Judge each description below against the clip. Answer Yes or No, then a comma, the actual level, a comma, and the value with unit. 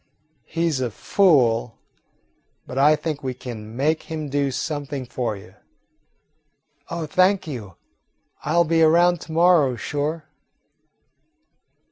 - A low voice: No, medium, 150 Hz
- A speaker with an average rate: No, slow, 125 wpm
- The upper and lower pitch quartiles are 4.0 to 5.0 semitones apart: Yes, average, 4.5 semitones